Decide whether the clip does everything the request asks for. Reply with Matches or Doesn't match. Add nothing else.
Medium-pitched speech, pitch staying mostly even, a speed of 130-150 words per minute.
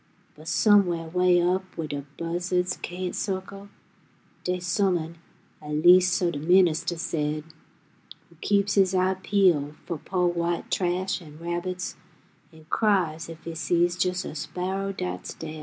Matches